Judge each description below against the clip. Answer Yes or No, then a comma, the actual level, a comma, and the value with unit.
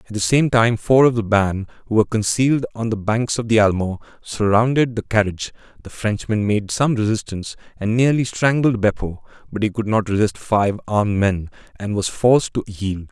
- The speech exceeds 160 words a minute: Yes, average, 190 wpm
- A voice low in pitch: Yes, low, 110 Hz